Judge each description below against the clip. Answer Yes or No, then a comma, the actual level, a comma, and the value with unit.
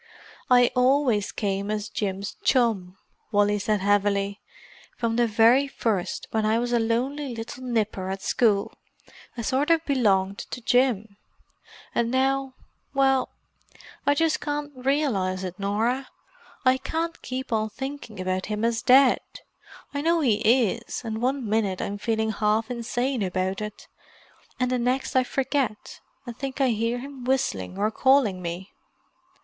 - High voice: Yes, high, 230 Hz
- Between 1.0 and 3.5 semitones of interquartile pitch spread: No, average, 4.2 semitones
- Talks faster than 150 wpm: No, average, 145 wpm